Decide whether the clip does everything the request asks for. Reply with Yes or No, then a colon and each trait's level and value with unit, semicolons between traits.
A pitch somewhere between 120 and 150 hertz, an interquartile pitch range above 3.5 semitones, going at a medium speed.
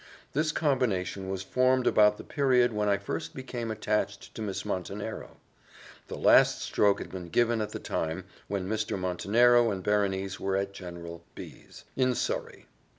No: low, 105 Hz; average, 3.9 semitones; average, 165 wpm